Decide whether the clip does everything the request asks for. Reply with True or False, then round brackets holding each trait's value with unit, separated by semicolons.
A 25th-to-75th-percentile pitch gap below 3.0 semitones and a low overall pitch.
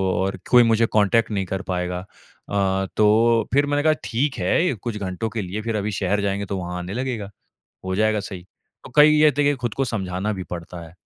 False (3.8 semitones; 105 Hz)